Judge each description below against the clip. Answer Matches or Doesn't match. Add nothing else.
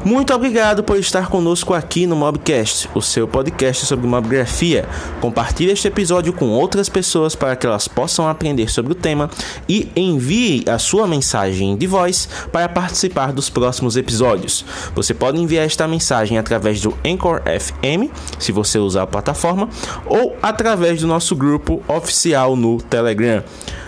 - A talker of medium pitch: Matches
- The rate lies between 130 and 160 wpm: Matches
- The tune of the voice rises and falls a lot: Matches